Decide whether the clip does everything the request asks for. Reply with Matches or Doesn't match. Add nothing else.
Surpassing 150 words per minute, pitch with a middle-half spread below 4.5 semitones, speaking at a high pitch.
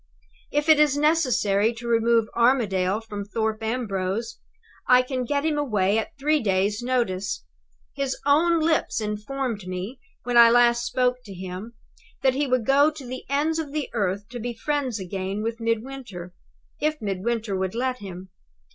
Doesn't match